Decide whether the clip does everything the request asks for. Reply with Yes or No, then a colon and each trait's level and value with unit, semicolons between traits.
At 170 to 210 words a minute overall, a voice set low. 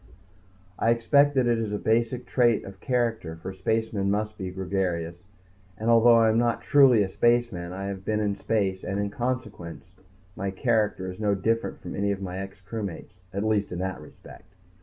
Yes: average, 180 wpm; low, 105 Hz